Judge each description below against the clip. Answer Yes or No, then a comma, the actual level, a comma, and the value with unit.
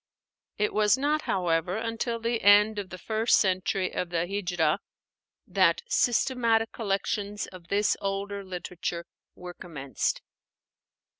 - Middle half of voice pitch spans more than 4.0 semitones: No, average, 3.7 semitones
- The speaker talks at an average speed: No, slow, 125 wpm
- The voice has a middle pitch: No, high, 200 Hz